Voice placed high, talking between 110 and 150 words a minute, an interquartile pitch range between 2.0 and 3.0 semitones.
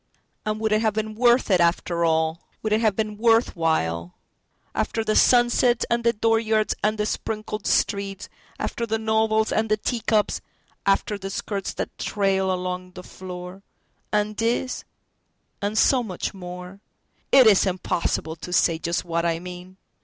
No: high, 210 Hz; average, 145 wpm; average, 3.4 semitones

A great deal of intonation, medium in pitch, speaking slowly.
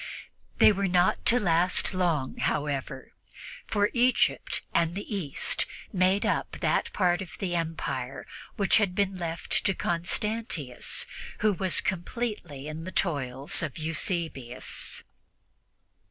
No: average, 4.1 semitones; medium, 175 Hz; slow, 125 wpm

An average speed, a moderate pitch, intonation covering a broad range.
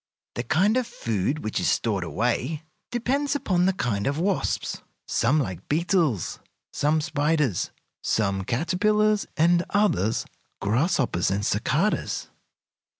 No: slow, 120 wpm; medium, 150 Hz; wide, 9.0 semitones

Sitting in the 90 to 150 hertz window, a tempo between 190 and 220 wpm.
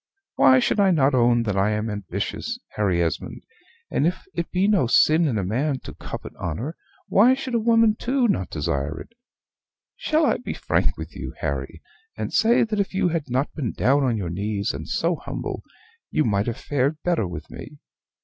Yes: low, 135 Hz; average, 195 wpm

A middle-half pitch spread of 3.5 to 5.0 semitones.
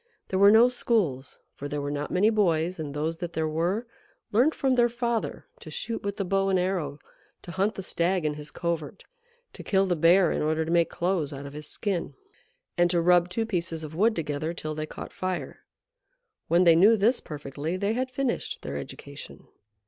Yes: average, 4.5 semitones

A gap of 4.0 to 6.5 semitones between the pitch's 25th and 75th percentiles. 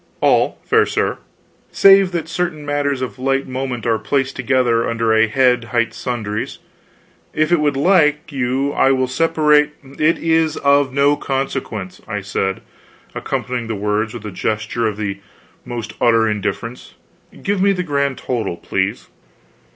Yes: average, 4.6 semitones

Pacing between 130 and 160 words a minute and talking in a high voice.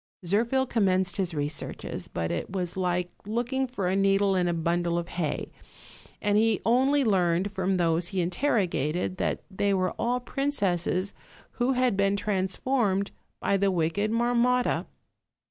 Yes: average, 150 wpm; high, 195 Hz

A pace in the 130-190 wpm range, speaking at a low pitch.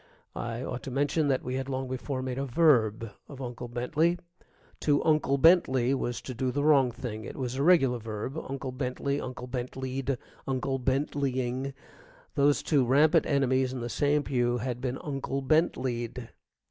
Yes: average, 150 wpm; low, 130 Hz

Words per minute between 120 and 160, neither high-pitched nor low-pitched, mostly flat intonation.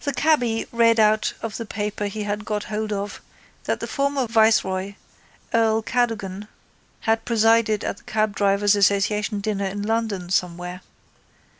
No: average, 145 wpm; high, 215 Hz; narrow, 2.0 semitones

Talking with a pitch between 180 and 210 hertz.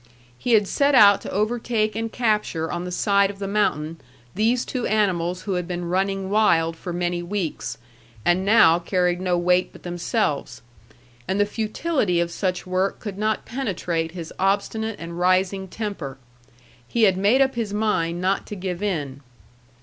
Yes: high, 190 Hz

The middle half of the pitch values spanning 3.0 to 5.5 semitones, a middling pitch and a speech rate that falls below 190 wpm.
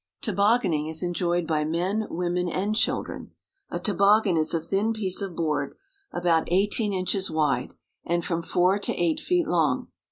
Yes: average, 3.5 semitones; medium, 180 Hz; average, 160 wpm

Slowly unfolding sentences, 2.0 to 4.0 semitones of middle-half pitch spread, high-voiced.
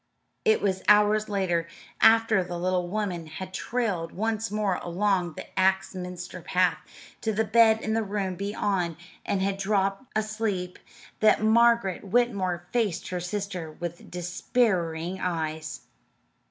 Yes: slow, 130 wpm; average, 3.3 semitones; high, 195 Hz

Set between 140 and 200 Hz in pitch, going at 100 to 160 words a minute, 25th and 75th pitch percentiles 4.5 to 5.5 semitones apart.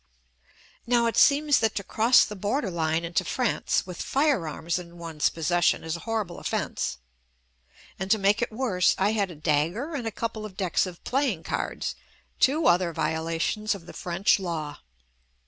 No: high, 190 Hz; average, 185 wpm; average, 5.2 semitones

